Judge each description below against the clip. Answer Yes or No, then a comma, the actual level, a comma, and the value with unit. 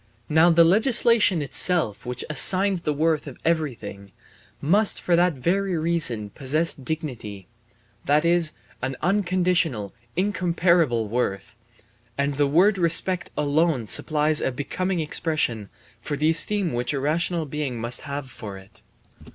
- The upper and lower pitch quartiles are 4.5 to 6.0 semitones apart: Yes, average, 4.9 semitones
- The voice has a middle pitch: Yes, medium, 155 Hz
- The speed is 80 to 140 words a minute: Yes, slow, 135 wpm